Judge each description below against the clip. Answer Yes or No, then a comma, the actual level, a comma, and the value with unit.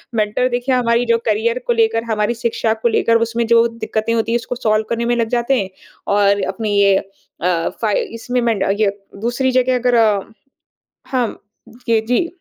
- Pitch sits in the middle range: No, high, 230 Hz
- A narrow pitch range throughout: Yes, narrow, 1.8 semitones